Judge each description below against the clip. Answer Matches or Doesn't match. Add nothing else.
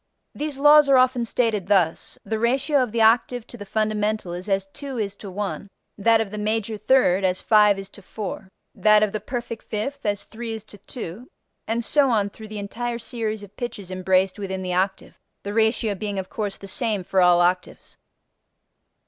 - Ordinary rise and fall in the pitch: Matches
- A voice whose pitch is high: Matches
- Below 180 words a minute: Doesn't match